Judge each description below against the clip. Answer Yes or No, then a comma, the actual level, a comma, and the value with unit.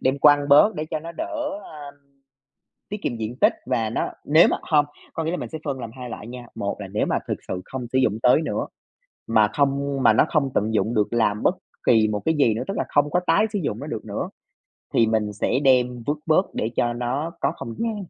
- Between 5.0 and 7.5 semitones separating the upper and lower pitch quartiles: Yes, average, 5.3 semitones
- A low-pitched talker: Yes, low, 130 Hz